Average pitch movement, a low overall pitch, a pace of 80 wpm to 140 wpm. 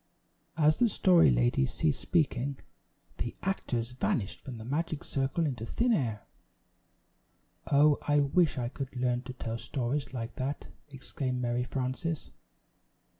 Yes: average, 3.6 semitones; low, 130 Hz; slow, 135 wpm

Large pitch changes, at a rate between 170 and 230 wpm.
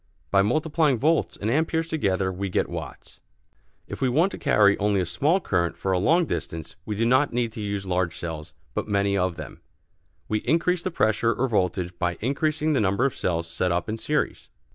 Yes: wide, 7.5 semitones; fast, 205 wpm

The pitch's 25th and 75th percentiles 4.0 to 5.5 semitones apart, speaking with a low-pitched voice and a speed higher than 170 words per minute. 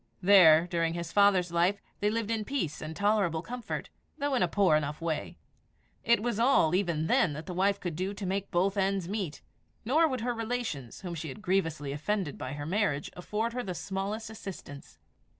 No: average, 4.5 semitones; high, 190 Hz; average, 195 wpm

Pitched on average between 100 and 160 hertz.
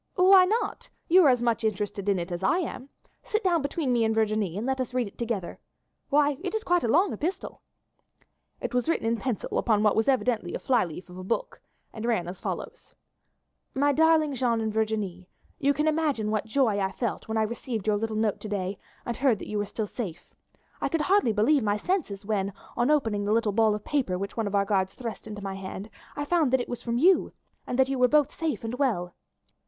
No: high, 230 Hz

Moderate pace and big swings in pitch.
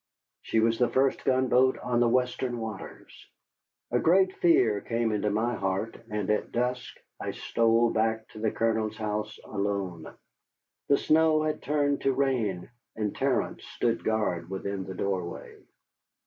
No: average, 150 wpm; average, 3.4 semitones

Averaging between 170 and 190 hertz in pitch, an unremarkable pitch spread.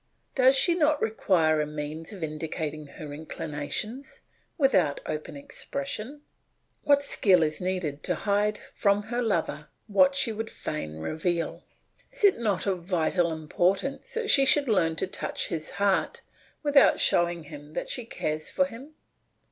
No: medium, 185 Hz; wide, 7.9 semitones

